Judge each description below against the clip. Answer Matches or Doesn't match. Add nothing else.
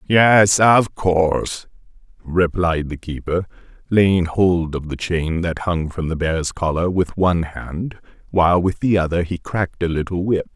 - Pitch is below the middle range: Matches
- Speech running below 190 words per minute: Matches